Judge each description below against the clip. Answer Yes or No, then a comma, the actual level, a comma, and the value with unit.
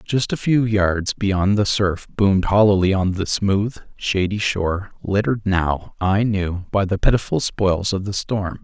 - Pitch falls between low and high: No, low, 100 Hz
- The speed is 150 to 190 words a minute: Yes, average, 175 wpm